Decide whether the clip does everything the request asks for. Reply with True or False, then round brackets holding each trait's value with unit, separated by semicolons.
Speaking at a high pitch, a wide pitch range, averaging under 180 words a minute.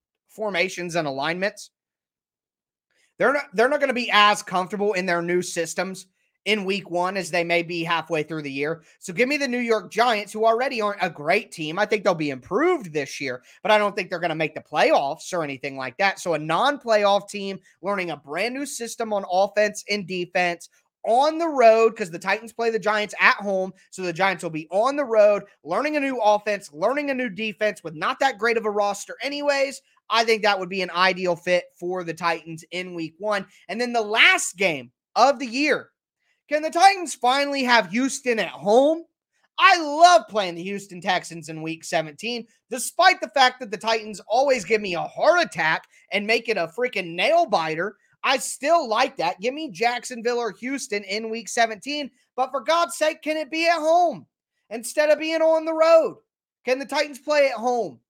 False (215 Hz; 6.6 semitones; 205 wpm)